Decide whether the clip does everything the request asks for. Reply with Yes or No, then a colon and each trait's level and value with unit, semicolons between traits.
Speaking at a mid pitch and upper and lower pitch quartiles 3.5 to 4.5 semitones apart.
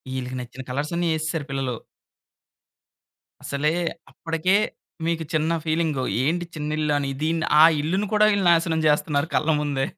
No: medium, 155 Hz; average, 2.7 semitones